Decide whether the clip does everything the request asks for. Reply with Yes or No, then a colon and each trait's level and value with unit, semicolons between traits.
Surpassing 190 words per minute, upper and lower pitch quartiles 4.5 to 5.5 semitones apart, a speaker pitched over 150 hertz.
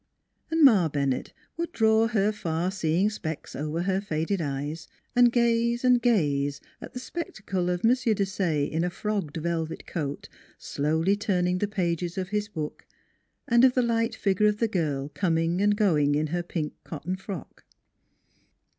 No: average, 165 wpm; average, 5.2 semitones; medium, 185 Hz